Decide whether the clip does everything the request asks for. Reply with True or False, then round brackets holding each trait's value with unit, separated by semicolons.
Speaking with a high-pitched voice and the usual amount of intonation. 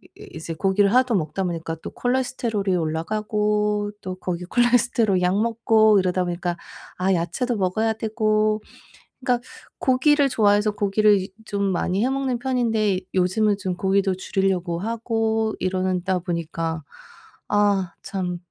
True (205 Hz; 3.4 semitones)